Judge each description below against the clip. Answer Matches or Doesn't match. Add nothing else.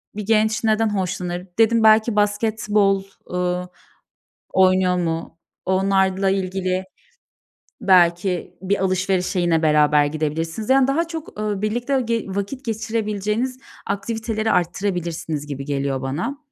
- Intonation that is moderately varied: Matches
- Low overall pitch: Doesn't match